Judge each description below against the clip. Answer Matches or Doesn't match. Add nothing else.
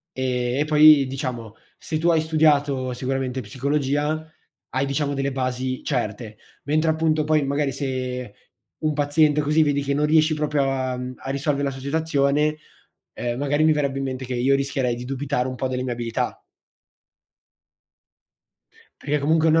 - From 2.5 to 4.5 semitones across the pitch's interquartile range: Matches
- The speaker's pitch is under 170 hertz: Matches